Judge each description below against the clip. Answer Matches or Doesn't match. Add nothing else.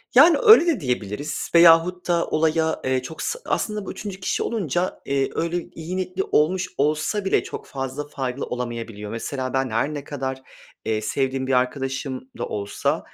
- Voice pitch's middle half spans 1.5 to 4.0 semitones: Doesn't match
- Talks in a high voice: Doesn't match